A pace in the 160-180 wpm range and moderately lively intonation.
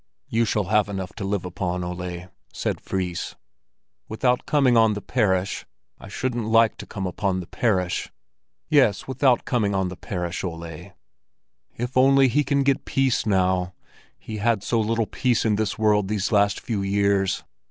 Yes: average, 165 wpm; average, 3.9 semitones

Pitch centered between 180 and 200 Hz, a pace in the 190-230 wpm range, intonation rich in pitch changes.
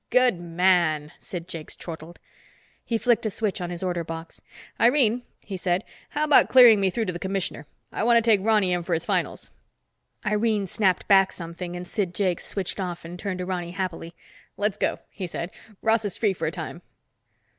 No: medium, 185 Hz; average, 195 wpm; average, 3.5 semitones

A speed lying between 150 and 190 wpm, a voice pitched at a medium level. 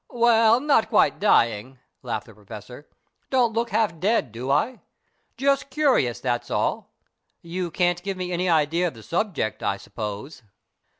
Yes: average, 155 wpm; medium, 175 Hz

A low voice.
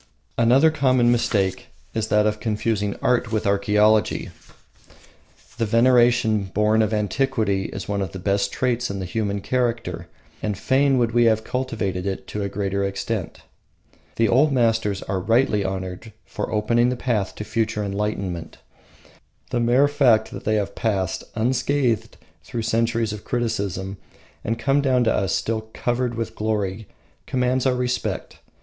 Yes: low, 110 Hz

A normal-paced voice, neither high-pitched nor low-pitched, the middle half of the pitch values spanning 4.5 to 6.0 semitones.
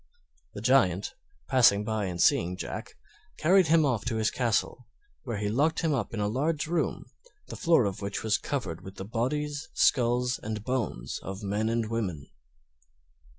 No: average, 165 wpm; low, 115 Hz; average, 5.3 semitones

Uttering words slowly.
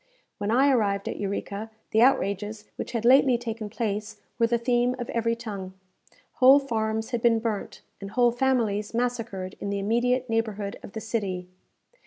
No: average, 170 wpm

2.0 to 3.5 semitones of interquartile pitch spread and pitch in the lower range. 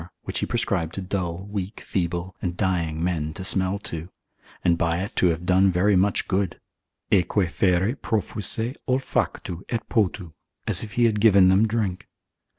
Yes: average, 2.9 semitones; very low, 95 Hz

